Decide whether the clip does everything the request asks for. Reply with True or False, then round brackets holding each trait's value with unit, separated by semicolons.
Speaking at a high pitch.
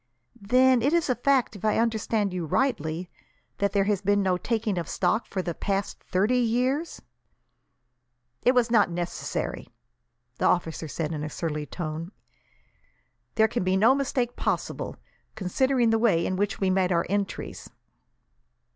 True (205 Hz)